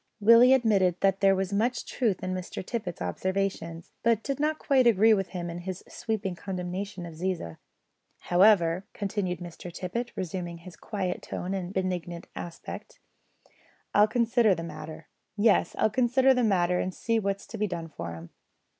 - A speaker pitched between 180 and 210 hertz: Yes, high, 190 Hz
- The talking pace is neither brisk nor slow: Yes, average, 165 wpm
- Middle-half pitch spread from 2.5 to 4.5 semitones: Yes, average, 3.8 semitones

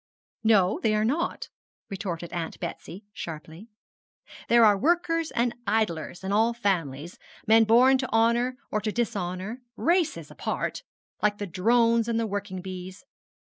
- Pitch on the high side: Yes, high, 215 Hz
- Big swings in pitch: No, average, 4.1 semitones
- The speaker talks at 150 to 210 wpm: No, average, 140 wpm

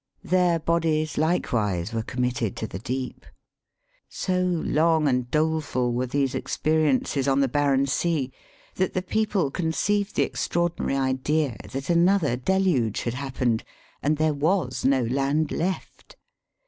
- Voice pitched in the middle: Yes, medium, 145 Hz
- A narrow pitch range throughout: No, average, 4.7 semitones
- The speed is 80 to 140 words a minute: Yes, slow, 135 wpm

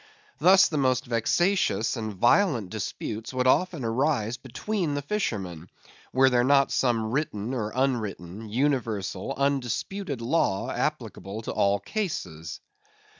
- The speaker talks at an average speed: No, slow, 125 wpm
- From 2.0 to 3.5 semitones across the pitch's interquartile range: No, average, 5.1 semitones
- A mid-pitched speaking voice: No, low, 125 Hz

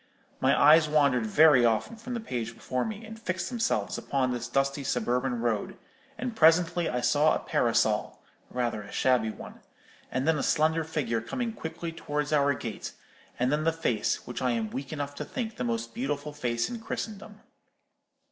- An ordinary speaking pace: Yes, average, 180 wpm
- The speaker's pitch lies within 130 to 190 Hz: Yes, medium, 140 Hz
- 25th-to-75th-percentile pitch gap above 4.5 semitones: Yes, average, 5.3 semitones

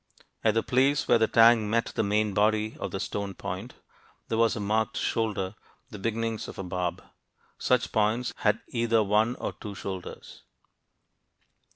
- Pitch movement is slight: Yes, narrow, 2.1 semitones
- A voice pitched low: Yes, low, 110 Hz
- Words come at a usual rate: Yes, average, 165 wpm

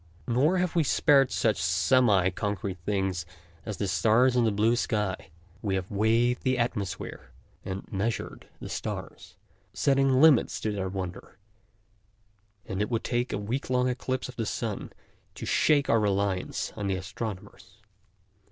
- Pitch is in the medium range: No, low, 110 Hz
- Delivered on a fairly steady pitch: No, average, 4.5 semitones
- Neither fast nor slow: Yes, average, 150 wpm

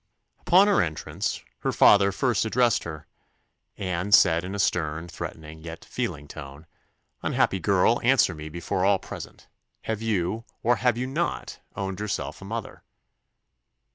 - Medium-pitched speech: No, very low, 95 Hz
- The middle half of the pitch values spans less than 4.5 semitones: No, wide, 5.5 semitones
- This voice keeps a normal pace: Yes, average, 145 wpm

